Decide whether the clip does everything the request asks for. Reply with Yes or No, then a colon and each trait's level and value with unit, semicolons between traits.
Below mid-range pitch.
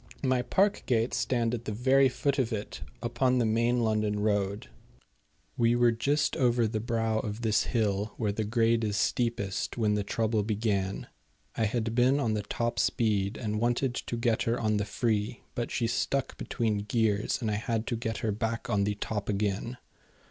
Yes: low, 115 Hz